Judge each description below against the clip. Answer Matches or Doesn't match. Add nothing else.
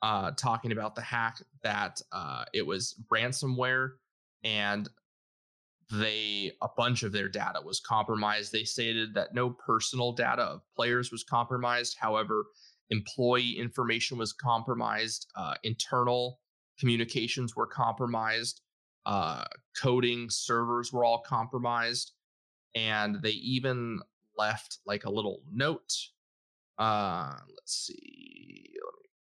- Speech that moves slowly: Matches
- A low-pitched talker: Matches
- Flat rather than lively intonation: Matches